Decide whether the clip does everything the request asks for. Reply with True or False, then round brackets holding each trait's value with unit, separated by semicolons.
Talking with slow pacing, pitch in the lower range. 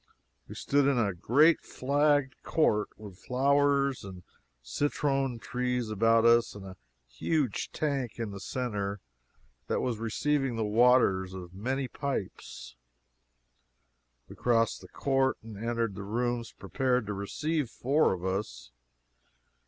True (130 wpm; 120 Hz)